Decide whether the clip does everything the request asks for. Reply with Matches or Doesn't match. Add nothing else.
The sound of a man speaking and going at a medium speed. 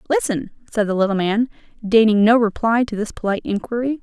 Doesn't match